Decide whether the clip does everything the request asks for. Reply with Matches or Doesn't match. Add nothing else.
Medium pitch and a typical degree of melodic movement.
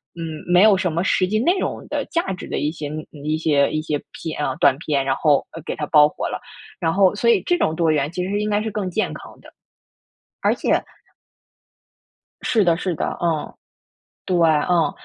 Matches